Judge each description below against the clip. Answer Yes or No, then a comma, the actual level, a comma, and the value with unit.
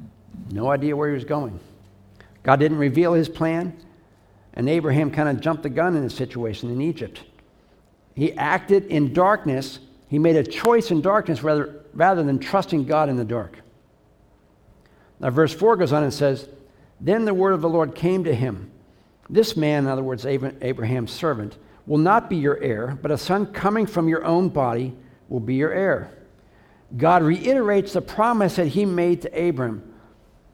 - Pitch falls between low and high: Yes, medium, 145 Hz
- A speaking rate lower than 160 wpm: No, average, 175 wpm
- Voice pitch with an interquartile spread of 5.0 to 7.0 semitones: Yes, wide, 5.5 semitones